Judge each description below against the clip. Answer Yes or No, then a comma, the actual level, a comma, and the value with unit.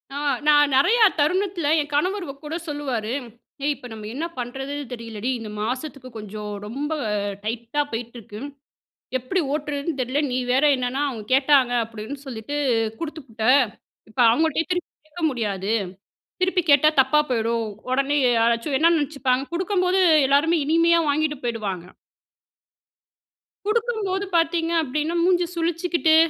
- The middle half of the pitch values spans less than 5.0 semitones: No, wide, 5.6 semitones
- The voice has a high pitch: Yes, very high, 285 Hz